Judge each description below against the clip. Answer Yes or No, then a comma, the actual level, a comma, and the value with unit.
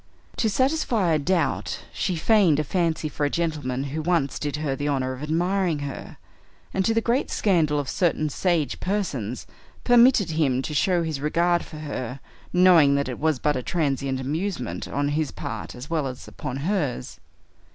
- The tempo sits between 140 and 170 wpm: No, average, 180 wpm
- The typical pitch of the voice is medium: Yes, medium, 155 Hz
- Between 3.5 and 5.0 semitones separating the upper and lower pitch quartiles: Yes, average, 4.3 semitones